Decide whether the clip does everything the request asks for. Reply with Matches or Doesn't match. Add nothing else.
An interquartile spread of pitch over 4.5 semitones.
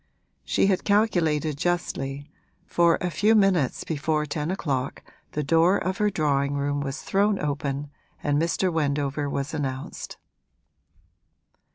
Doesn't match